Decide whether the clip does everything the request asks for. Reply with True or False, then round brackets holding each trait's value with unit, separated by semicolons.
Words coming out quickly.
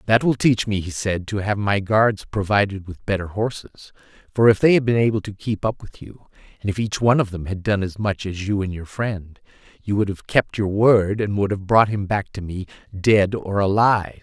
True (240 wpm)